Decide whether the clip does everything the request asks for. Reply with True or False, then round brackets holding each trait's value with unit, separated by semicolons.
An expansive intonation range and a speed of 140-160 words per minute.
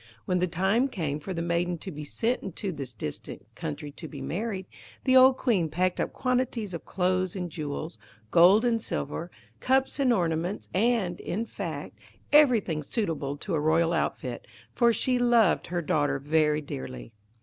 False (6.6 semitones; 170 wpm)